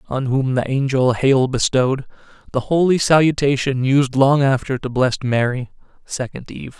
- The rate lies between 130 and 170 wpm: Yes, average, 150 wpm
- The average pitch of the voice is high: No, low, 135 Hz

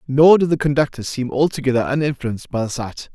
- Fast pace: No, average, 190 wpm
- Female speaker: No, male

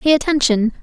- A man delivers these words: No, female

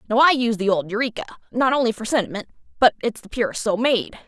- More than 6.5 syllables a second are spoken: Yes, 7.0 syllables/s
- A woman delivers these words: Yes, female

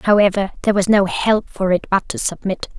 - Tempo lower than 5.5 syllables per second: No, 5.6 syllables/s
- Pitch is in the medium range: No, high, 195 Hz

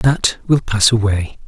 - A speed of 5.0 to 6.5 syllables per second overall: No, 3.8 syllables/s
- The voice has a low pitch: Yes, low, 110 Hz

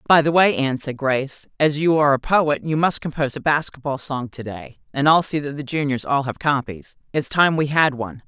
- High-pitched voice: No, medium, 145 Hz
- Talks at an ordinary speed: No, fast, 240 wpm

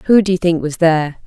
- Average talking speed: No, fast, 285 wpm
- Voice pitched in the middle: Yes, medium, 170 Hz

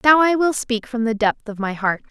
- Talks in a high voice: Yes, high, 240 Hz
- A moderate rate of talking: No, fast, 315 wpm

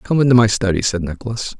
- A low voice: Yes, low, 110 Hz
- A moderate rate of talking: No, fast, 225 wpm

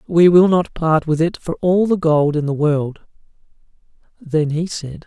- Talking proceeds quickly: No, average, 190 wpm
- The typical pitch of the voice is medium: Yes, medium, 165 Hz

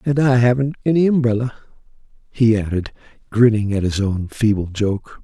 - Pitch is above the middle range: No, low, 115 Hz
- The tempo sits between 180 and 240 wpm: No, average, 150 wpm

